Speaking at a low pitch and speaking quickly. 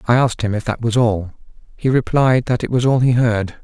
Yes: low, 120 Hz; fast, 250 wpm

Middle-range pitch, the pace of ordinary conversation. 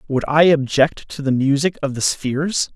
Yes: medium, 145 Hz; average, 195 wpm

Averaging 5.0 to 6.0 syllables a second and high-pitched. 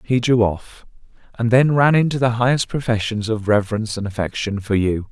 No: 5.5 syllables/s; low, 115 Hz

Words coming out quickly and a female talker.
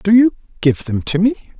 No: fast, 225 wpm; male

